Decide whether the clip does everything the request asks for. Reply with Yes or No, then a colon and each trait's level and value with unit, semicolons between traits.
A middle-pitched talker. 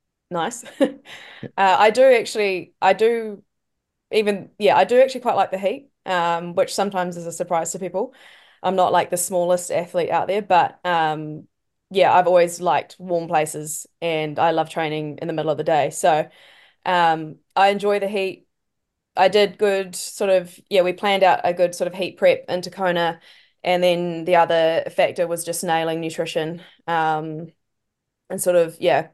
Yes: medium, 180 Hz